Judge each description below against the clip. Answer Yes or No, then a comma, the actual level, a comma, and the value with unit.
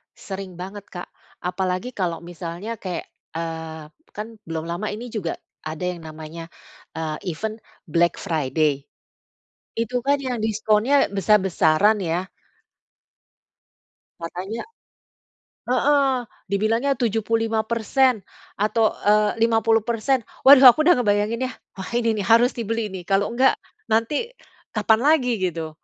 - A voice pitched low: No, high, 210 Hz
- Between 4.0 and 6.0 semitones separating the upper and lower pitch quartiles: Yes, average, 4.8 semitones